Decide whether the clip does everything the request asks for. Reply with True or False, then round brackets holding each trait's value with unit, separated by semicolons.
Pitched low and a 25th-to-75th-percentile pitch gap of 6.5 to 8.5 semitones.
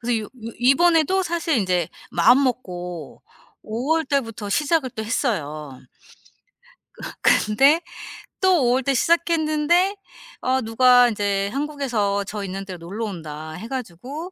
False (245 Hz; 6.8 semitones)